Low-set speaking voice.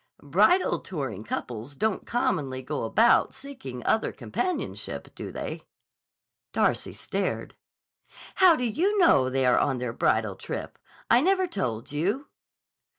No: medium, 155 Hz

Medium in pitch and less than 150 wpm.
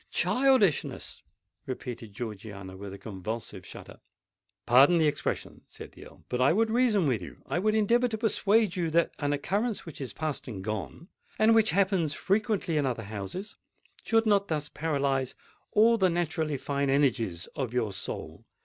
No: medium, 150 Hz; average, 165 wpm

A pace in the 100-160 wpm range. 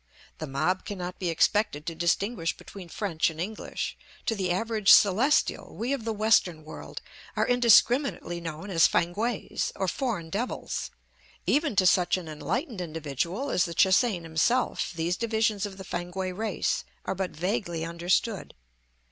Yes: average, 155 wpm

